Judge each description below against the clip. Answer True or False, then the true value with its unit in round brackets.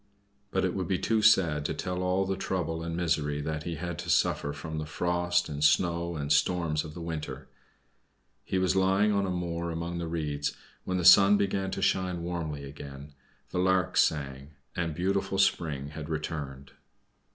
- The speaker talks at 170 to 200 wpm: True (185 wpm)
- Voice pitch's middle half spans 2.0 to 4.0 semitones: True (3.4 semitones)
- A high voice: False (85 Hz)